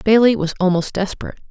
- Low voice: No, high, 200 Hz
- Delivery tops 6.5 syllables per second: Yes, 7.3 syllables/s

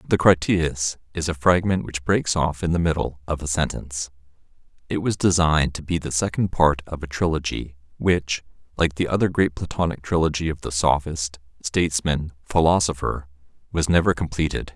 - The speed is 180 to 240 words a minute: No, average, 165 wpm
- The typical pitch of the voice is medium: No, very low, 80 Hz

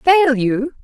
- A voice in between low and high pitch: No, very high, 275 Hz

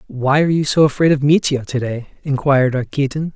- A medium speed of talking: Yes, average, 195 wpm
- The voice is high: No, medium, 140 Hz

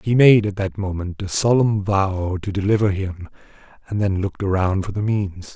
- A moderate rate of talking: Yes, average, 195 wpm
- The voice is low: Yes, low, 100 Hz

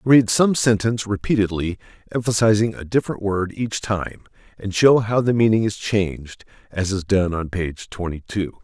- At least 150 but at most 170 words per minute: Yes, average, 165 wpm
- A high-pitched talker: No, low, 105 Hz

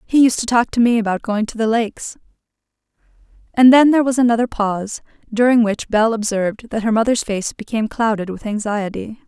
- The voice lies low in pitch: No, high, 225 Hz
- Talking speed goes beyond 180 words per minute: Yes, average, 190 wpm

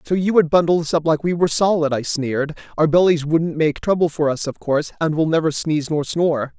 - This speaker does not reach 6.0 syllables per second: No, 6.1 syllables/s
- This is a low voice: No, medium, 160 Hz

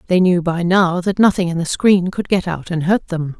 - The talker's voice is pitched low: No, medium, 180 Hz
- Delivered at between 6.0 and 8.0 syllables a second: No, 5.0 syllables/s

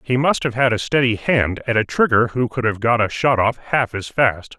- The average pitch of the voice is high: No, low, 120 Hz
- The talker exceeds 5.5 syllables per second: No, 5.0 syllables/s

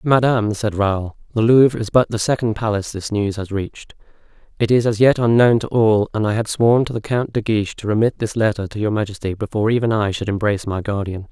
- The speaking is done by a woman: No, male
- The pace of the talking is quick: Yes, fast, 235 wpm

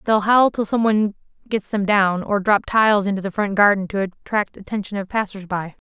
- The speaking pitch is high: Yes, high, 200 Hz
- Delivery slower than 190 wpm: No, fast, 205 wpm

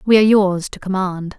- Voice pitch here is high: Yes, high, 195 Hz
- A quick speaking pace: Yes, fast, 215 wpm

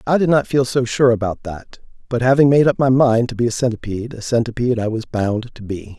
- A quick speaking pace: Yes, fast, 250 wpm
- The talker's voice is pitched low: Yes, low, 120 Hz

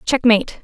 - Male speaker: No, female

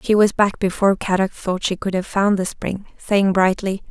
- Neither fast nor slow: No, fast, 215 wpm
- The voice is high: Yes, high, 195 Hz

